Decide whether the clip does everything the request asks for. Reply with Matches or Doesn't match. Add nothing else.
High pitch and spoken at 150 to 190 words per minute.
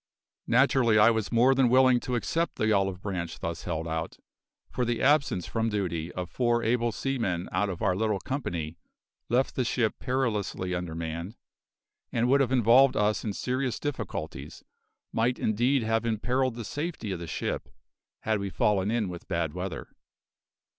Doesn't match